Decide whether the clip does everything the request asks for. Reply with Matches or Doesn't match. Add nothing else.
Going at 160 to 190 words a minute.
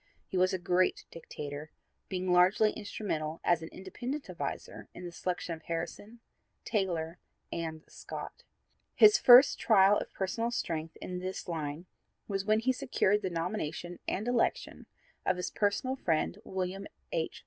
Doesn't match